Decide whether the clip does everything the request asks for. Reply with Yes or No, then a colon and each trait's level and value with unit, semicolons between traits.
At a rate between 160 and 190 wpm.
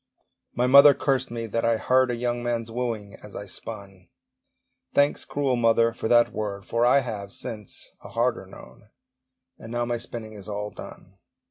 Yes: average, 175 wpm